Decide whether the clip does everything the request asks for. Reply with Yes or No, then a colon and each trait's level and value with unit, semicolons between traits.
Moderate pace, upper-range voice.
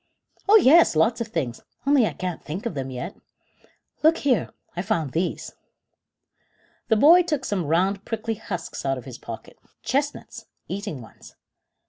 Yes: average, 155 wpm; high, 200 Hz